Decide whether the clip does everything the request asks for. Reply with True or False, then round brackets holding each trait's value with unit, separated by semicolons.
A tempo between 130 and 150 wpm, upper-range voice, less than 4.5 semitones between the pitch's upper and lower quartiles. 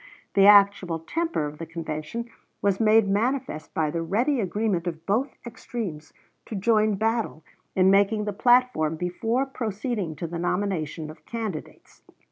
False (145 wpm; 200 Hz; 5.4 semitones)